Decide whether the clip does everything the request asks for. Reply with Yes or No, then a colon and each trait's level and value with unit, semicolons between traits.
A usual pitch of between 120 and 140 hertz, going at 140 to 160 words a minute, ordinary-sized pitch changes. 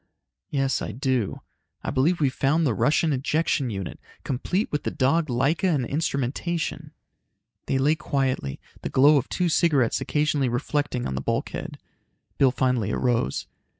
Yes: low, 135 Hz; average, 150 wpm; average, 3.3 semitones